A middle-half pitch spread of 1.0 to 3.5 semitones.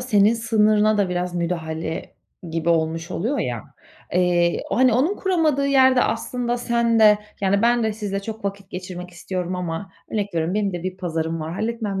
No: average, 4.8 semitones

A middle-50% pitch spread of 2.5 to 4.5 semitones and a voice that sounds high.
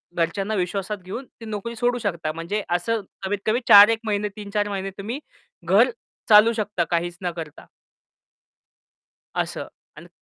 Yes: average, 3.5 semitones; high, 205 Hz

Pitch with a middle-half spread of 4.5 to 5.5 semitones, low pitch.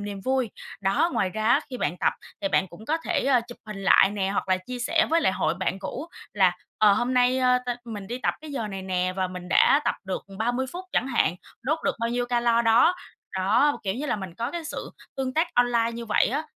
No: average, 5.1 semitones; high, 235 Hz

